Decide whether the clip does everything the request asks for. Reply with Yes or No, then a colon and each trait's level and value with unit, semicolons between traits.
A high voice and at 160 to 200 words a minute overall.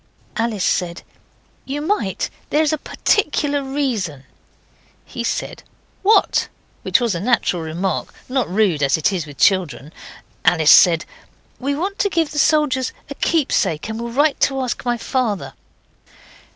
No: high, 235 Hz; average, 145 wpm